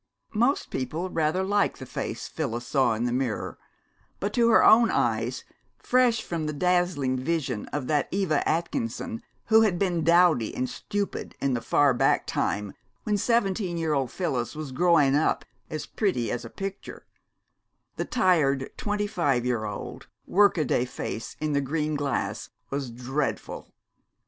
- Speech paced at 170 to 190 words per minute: No, average, 155 wpm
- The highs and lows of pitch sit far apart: Yes, wide, 6.4 semitones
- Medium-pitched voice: Yes, medium, 155 Hz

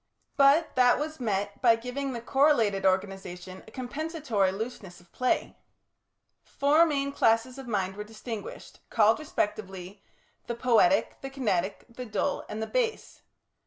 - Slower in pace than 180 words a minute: Yes, average, 140 wpm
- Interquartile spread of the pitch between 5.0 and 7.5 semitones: Yes, average, 5.3 semitones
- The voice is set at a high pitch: Yes, high, 230 Hz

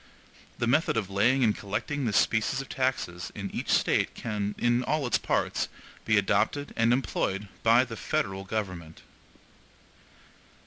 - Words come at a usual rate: Yes, average, 145 wpm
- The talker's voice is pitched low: Yes, low, 115 Hz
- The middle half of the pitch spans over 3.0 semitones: Yes, average, 4.3 semitones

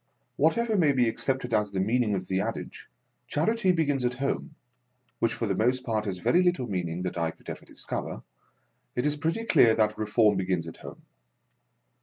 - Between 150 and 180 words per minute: No, average, 195 wpm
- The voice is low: Yes, low, 120 Hz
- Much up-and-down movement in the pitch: Yes, wide, 6.4 semitones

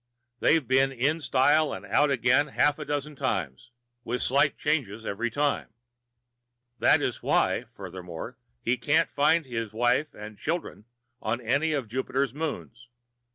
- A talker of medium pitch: No, low, 130 Hz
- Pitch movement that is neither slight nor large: Yes, average, 4.1 semitones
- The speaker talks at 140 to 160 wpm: Yes, average, 145 wpm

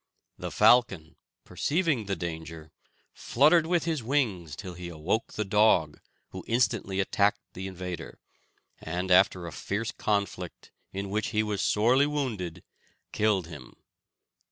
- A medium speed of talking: No, slow, 130 wpm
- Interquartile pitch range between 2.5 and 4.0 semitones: No, average, 4.7 semitones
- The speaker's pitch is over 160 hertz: No, low, 100 Hz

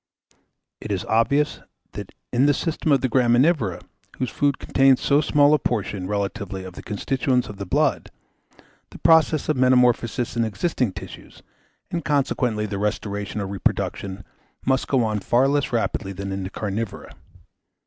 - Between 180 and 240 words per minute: No, average, 160 wpm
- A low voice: Yes, low, 120 Hz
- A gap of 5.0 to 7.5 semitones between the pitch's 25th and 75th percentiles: Yes, average, 5.3 semitones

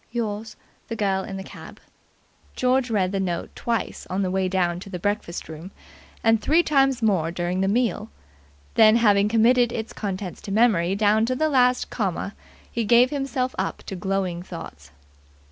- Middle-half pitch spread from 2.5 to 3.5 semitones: No, average, 4.1 semitones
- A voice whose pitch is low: No, high, 205 Hz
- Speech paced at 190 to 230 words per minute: No, average, 175 wpm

